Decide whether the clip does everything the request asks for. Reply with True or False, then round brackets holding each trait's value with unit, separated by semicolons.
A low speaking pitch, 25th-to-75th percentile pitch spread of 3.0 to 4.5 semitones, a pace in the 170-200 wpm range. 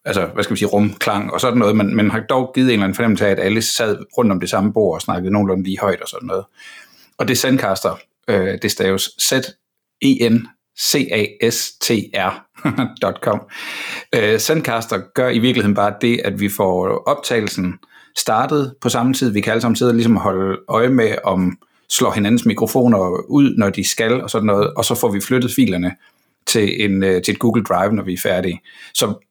True (110 Hz; 3.9 semitones; 195 wpm)